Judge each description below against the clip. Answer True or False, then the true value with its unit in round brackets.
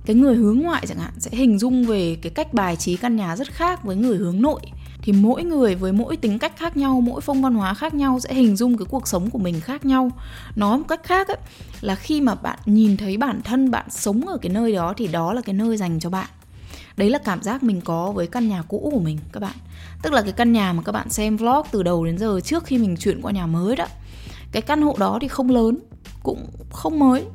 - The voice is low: False (220 Hz)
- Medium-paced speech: False (265 wpm)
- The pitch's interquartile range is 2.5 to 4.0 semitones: False (5.5 semitones)